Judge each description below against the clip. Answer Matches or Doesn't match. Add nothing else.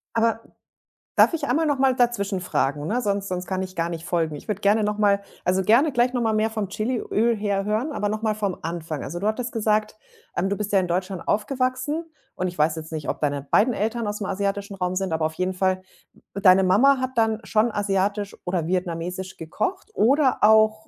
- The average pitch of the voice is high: Matches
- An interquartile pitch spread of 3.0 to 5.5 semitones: Matches